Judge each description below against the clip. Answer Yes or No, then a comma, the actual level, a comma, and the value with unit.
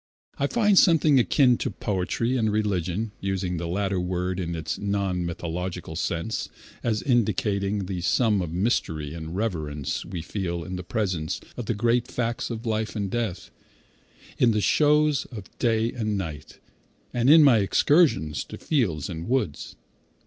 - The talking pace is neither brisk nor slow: Yes, average, 155 wpm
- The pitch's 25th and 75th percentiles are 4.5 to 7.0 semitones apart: Yes, average, 5.0 semitones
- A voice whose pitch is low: Yes, low, 100 Hz